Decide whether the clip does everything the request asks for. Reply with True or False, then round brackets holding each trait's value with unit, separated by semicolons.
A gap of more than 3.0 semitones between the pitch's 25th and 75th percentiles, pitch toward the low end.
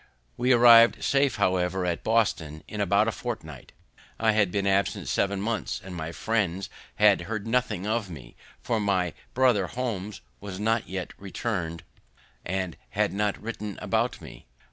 True (3.6 semitones; 100 Hz)